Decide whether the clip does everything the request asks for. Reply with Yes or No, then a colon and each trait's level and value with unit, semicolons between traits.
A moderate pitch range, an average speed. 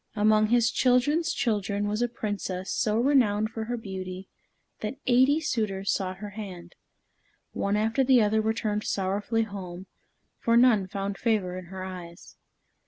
Yes: average, 3.3 semitones; average, 150 wpm